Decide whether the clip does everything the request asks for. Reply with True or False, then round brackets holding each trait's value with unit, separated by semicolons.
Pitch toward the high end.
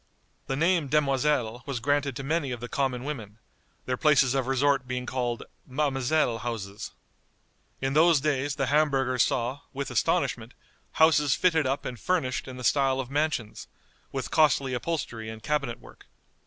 False (135 Hz)